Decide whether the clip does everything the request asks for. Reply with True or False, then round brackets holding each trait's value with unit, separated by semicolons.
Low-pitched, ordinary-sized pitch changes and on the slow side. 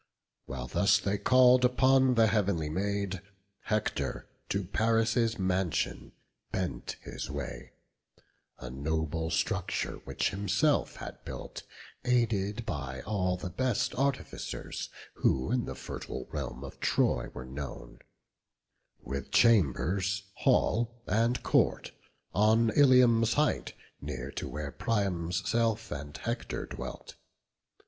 False (100 Hz; 5.8 semitones; 115 wpm)